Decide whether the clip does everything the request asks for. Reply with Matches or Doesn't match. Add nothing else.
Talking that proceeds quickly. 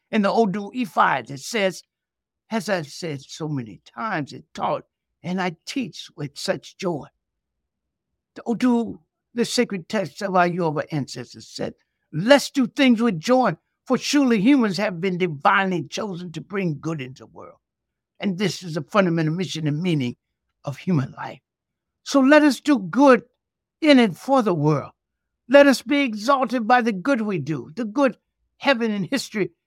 Doesn't match